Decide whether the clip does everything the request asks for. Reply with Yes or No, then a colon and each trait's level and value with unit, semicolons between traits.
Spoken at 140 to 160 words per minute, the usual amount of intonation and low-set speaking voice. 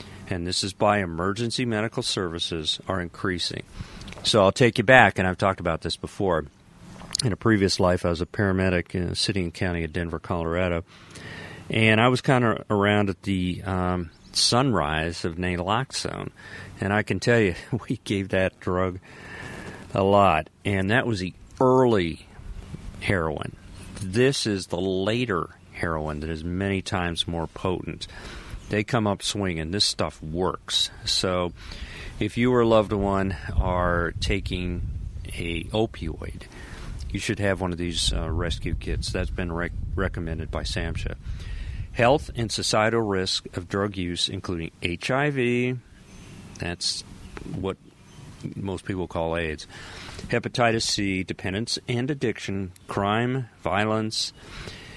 Yes: average, 145 wpm; average, 3.6 semitones; very low, 95 Hz